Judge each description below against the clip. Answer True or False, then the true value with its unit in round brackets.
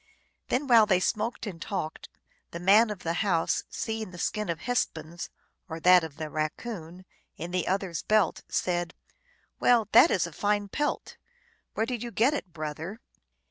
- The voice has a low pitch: False (185 Hz)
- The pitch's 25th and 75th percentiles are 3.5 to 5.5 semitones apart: True (4.8 semitones)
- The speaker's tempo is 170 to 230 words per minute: True (180 wpm)